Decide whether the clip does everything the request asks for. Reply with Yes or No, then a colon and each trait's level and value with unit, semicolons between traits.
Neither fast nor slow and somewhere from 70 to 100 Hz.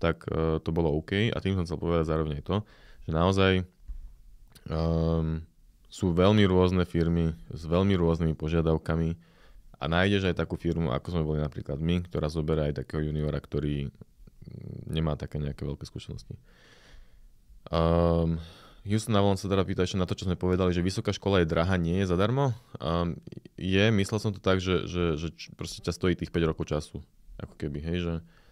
No: fast, 175 wpm; very low, 85 Hz